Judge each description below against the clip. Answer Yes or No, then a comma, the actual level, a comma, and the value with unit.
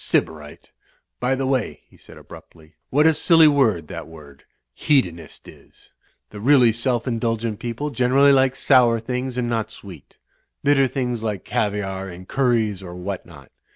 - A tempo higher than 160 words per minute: No, average, 155 wpm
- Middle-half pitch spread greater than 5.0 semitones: Yes, wide, 5.5 semitones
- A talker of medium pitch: No, low, 115 Hz